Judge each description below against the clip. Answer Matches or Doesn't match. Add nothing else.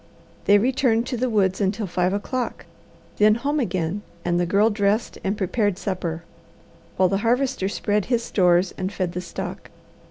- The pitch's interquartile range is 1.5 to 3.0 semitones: Doesn't match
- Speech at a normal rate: Matches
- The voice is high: Matches